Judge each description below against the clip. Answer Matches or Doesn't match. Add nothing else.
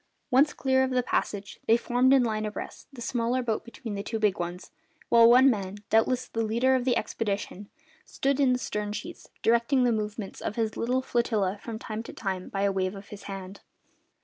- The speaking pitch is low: Doesn't match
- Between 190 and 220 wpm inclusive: Matches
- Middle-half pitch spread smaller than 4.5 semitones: Matches